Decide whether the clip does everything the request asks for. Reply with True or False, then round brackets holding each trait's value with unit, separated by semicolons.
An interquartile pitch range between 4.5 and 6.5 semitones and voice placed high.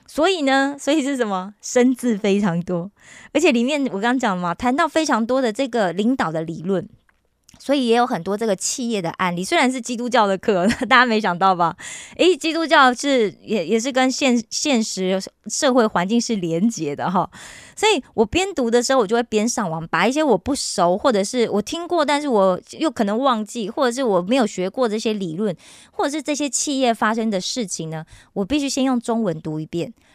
True (5.5 semitones; 235 Hz)